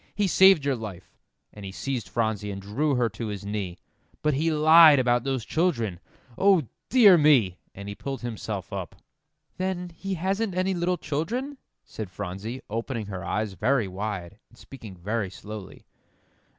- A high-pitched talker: No, low, 120 Hz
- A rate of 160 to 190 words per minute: Yes, average, 165 wpm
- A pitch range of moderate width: No, wide, 8.1 semitones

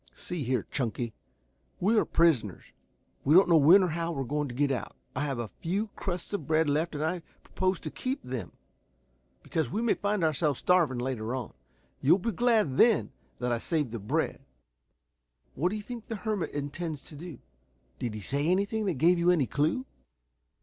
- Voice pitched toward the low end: No, medium, 160 Hz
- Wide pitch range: Yes, wide, 5.7 semitones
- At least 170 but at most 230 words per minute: Yes, average, 195 wpm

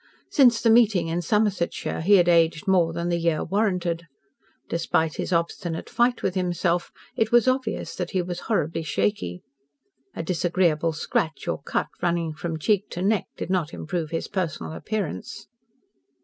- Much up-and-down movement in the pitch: No, average, 3.3 semitones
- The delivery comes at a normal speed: Yes, average, 160 wpm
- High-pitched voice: No, medium, 175 Hz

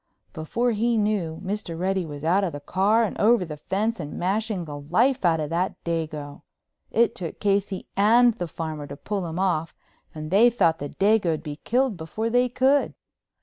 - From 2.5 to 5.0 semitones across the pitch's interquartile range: No, wide, 5.5 semitones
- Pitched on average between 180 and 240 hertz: Yes, high, 190 Hz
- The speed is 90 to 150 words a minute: No, average, 190 wpm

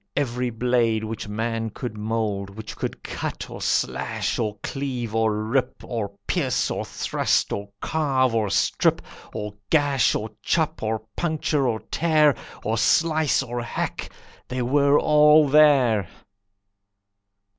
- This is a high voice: No, low, 120 Hz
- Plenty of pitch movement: No, average, 4.5 semitones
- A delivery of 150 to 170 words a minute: No, slow, 135 wpm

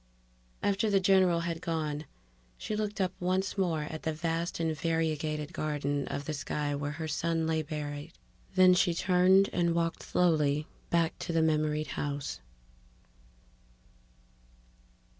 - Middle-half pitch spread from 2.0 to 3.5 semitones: Yes, average, 2.9 semitones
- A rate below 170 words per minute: Yes, average, 140 wpm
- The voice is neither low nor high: Yes, medium, 160 Hz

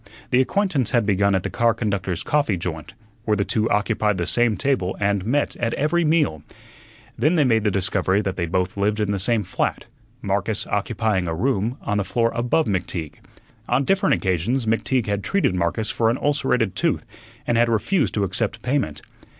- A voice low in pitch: Yes, low, 110 Hz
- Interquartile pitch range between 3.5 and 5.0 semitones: Yes, average, 4.4 semitones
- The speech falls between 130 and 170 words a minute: No, average, 190 wpm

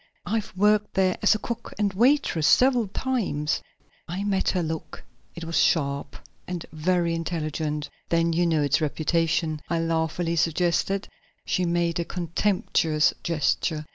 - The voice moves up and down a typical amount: Yes, average, 3.0 semitones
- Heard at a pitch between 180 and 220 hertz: No, medium, 170 Hz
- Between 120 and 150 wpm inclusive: Yes, average, 140 wpm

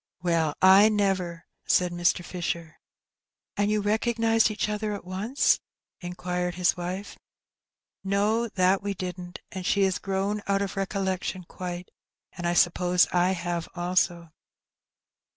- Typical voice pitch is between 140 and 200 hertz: Yes, medium, 185 Hz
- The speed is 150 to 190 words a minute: No, slow, 135 wpm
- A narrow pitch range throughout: Yes, narrow, 2.3 semitones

